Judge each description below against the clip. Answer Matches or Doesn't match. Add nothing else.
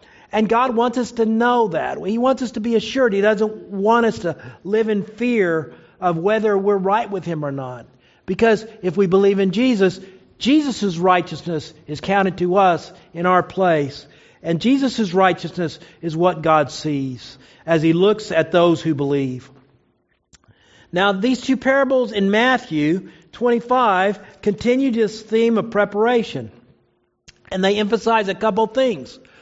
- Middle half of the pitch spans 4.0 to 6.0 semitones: Matches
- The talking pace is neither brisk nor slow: Matches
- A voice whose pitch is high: Matches